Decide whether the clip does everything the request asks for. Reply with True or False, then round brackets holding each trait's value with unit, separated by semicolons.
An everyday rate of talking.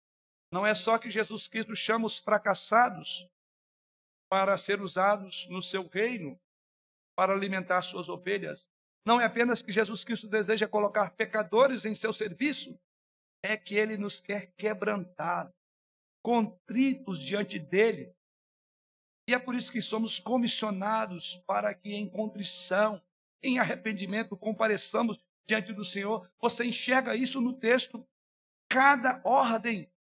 True (130 wpm)